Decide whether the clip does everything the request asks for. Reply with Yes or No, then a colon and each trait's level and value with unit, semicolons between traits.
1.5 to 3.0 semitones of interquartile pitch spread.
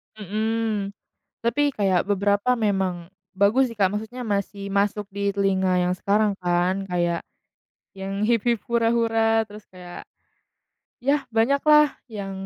Yes: average, 2.7 semitones